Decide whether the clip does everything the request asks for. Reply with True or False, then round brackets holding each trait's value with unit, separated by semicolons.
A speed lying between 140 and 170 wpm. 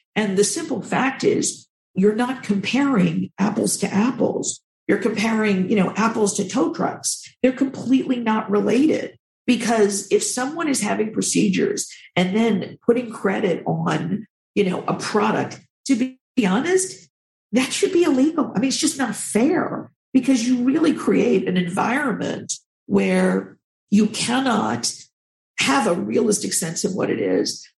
True (145 wpm)